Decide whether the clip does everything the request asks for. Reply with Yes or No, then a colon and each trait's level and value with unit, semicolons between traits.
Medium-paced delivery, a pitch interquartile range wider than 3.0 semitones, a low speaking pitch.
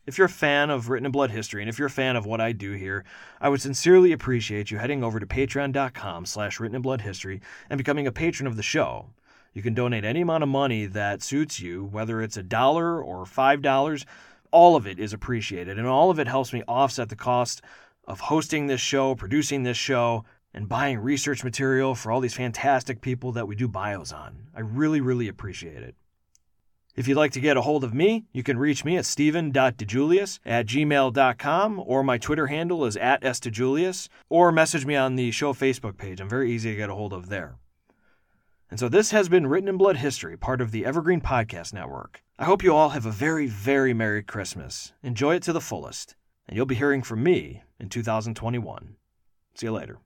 No: fast, 210 wpm; average, 4.5 semitones; low, 130 Hz